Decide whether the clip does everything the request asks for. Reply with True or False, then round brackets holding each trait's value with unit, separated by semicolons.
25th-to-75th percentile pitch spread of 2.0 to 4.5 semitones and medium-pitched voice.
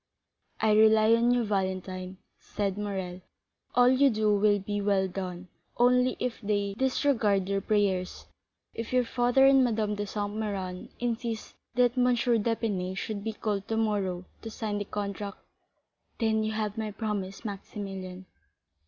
False (2.6 semitones; 210 Hz)